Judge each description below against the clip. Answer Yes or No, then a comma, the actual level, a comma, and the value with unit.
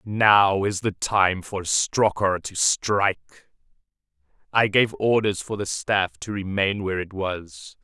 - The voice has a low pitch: Yes, low, 100 Hz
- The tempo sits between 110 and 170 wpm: Yes, average, 145 wpm